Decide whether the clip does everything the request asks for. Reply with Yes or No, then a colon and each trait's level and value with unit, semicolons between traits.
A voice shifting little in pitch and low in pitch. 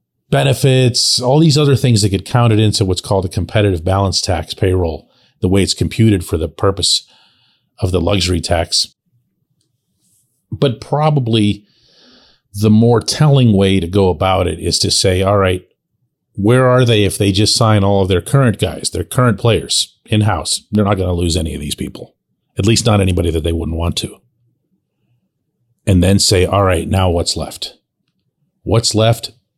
No: average, 4.1 semitones; low, 100 Hz